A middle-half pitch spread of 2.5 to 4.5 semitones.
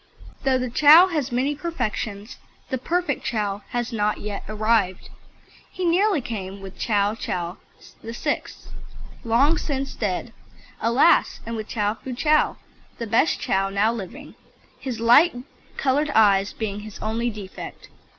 No: average, 4.9 semitones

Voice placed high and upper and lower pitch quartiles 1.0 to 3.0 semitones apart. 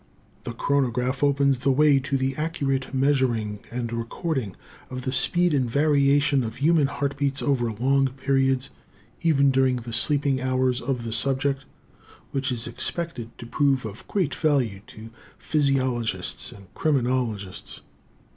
No: low, 135 Hz; average, 2.7 semitones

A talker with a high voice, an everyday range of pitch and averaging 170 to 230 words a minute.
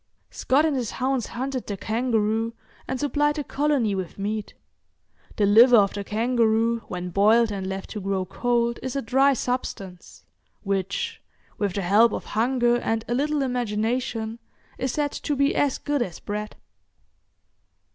No: high, 230 Hz; average, 3.9 semitones; average, 155 wpm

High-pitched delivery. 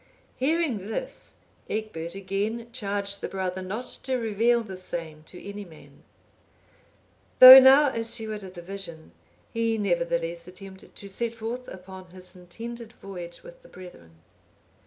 Yes: high, 200 Hz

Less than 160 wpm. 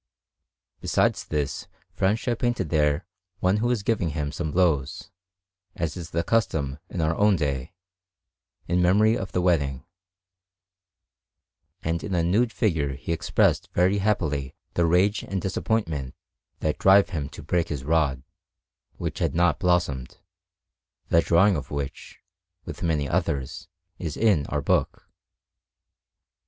Yes: slow, 135 wpm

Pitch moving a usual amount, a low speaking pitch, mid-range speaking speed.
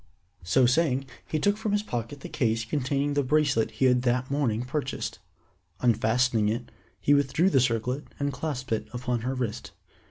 Yes: average, 3.1 semitones; low, 130 Hz; average, 170 wpm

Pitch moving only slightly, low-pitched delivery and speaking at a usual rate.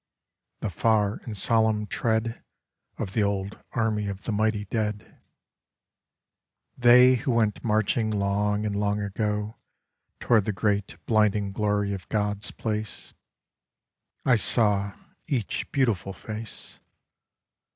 No: narrow, 1.5 semitones; low, 105 Hz; slow, 120 wpm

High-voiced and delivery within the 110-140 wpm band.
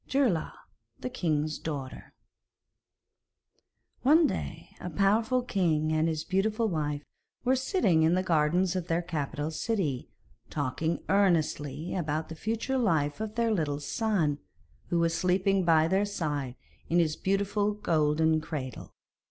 No: medium, 170 Hz; slow, 135 wpm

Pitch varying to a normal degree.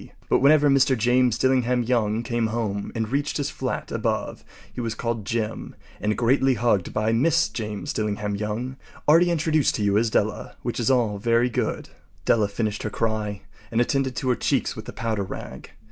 Yes: average, 3.3 semitones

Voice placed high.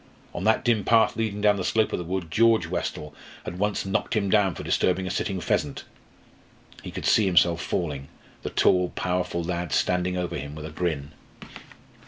No: very low, 90 Hz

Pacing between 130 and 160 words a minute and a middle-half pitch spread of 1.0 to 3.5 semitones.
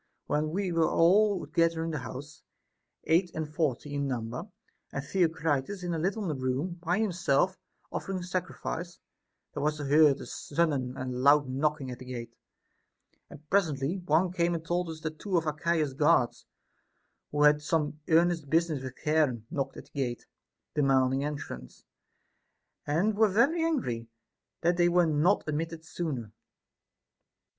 No: average, 155 wpm; average, 3.9 semitones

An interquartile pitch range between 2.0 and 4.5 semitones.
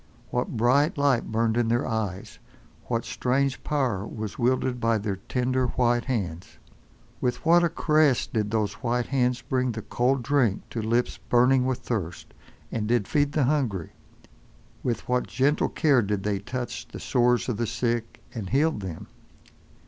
Yes: average, 2.9 semitones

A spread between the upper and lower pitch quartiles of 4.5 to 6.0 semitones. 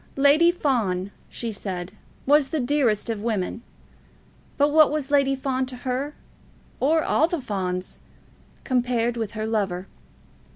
Yes: average, 5.1 semitones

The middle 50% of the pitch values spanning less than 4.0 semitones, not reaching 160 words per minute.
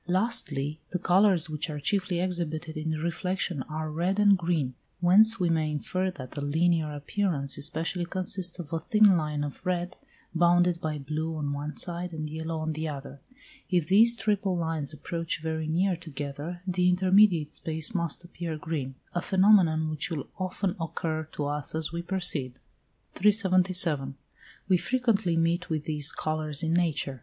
No: average, 3.0 semitones; average, 165 wpm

